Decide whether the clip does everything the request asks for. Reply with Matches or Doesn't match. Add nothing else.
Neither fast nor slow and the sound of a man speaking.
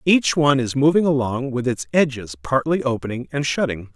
Matches